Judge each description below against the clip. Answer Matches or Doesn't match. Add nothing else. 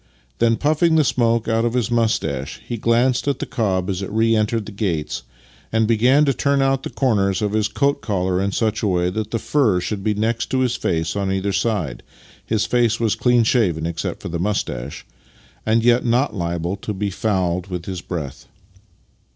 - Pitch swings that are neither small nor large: Matches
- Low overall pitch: Matches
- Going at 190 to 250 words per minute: Matches